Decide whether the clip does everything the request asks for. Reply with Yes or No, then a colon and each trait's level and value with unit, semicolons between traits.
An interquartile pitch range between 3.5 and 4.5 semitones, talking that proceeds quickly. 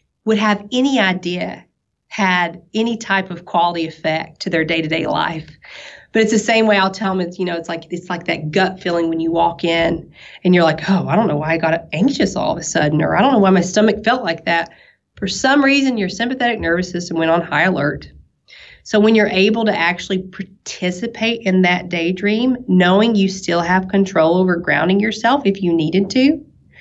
Yes: average, 4.2 semitones; fast, 210 wpm